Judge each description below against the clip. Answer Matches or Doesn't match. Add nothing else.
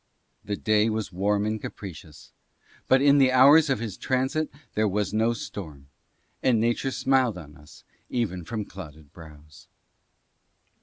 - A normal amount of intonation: Doesn't match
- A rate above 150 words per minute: Doesn't match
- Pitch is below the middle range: Matches